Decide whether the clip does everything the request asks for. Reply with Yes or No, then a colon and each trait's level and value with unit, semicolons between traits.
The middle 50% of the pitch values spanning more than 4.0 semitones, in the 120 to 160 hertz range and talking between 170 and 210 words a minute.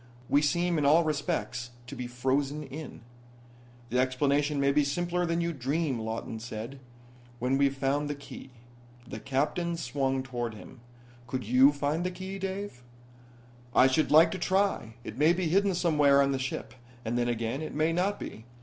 Yes: average, 4.5 semitones; medium, 140 Hz; average, 175 wpm